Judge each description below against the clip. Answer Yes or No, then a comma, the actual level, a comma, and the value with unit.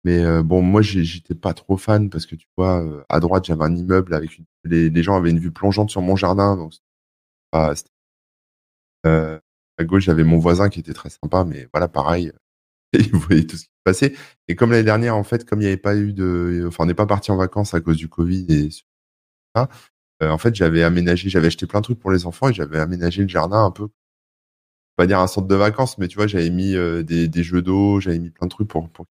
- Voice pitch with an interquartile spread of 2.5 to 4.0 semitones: Yes, average, 3.2 semitones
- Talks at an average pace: No, fast, 245 wpm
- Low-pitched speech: Yes, very low, 85 Hz